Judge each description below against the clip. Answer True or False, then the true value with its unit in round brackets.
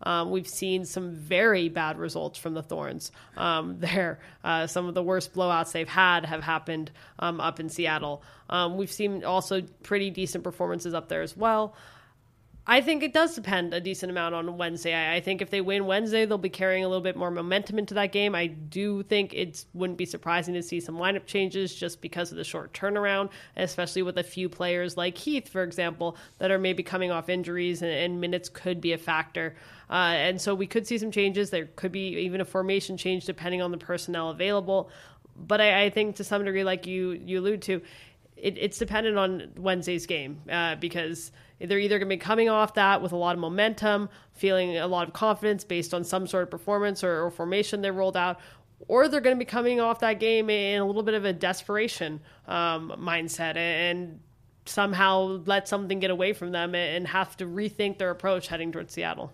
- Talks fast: True (210 wpm)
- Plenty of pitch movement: False (2.6 semitones)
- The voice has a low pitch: False (185 Hz)